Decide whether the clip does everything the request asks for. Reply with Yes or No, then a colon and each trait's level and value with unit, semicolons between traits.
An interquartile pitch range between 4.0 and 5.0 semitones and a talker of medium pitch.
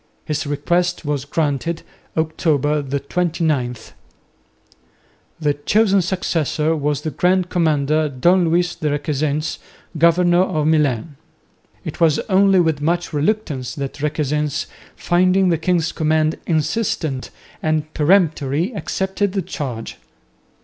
No: average, 3.1 semitones; medium, 155 Hz